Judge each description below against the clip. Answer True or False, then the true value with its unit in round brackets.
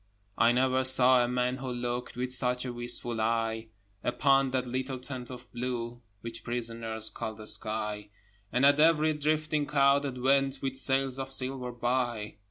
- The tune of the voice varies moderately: False (1.9 semitones)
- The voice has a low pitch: True (125 Hz)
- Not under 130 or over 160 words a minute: False (170 wpm)